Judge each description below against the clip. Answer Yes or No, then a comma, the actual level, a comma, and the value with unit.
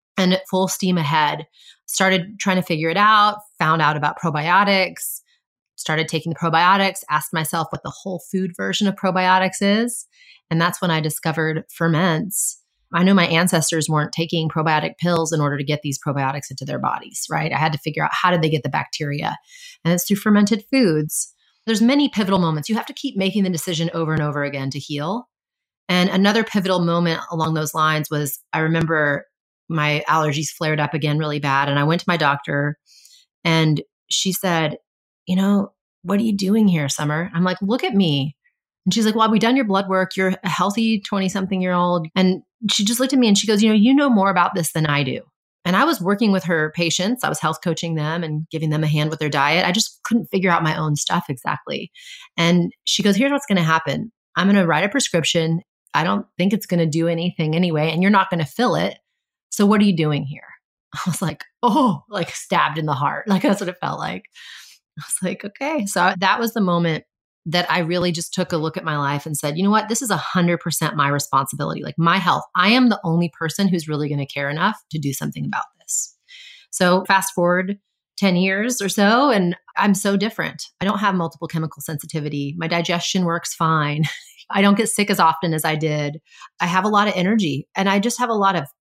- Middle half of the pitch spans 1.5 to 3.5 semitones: No, average, 4.0 semitones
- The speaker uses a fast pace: Yes, fast, 225 wpm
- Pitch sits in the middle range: Yes, medium, 175 Hz